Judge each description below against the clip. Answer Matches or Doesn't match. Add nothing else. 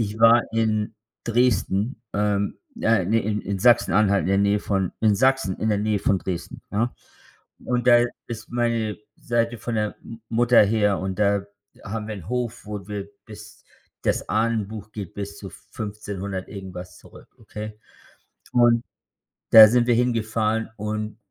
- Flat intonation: Matches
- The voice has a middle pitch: Doesn't match